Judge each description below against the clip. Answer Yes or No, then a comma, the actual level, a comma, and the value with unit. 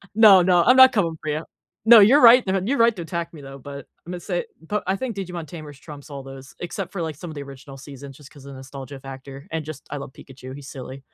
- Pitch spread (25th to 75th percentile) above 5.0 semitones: Yes, wide, 5.5 semitones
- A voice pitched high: No, medium, 155 Hz